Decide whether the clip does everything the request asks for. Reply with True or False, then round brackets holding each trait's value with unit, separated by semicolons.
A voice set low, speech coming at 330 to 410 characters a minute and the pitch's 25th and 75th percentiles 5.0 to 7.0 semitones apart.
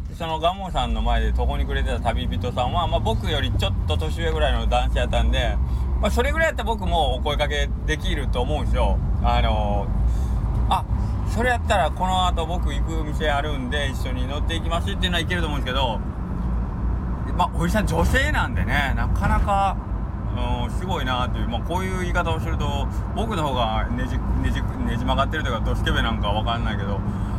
True (95 Hz; 405 characters per minute; 5.6 semitones)